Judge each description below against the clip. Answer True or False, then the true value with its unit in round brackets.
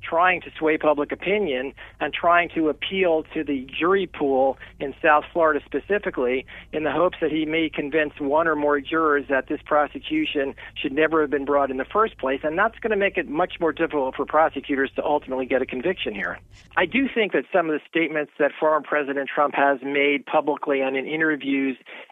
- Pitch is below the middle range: False (150 Hz)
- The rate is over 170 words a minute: True (205 wpm)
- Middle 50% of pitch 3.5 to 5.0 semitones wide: False (2.6 semitones)